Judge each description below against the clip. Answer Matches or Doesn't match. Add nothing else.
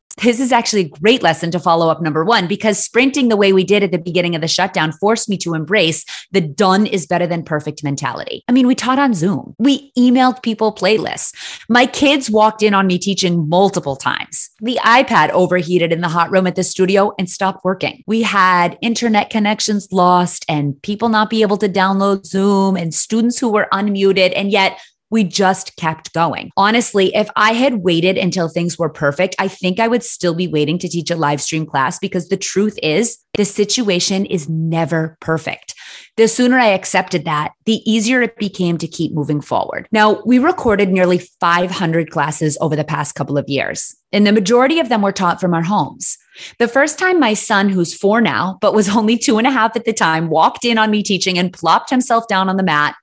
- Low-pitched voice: Doesn't match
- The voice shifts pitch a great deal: Doesn't match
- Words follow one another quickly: Matches